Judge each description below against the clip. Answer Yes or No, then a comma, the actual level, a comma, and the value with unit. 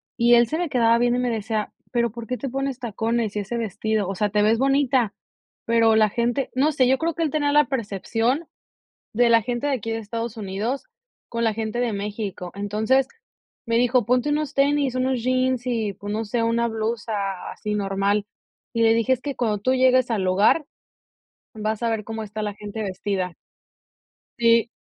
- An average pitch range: Yes, average, 3.2 semitones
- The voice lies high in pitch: Yes, high, 230 Hz